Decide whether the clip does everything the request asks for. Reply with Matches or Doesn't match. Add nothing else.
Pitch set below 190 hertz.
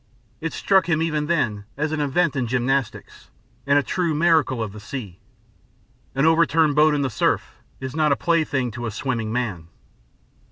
Matches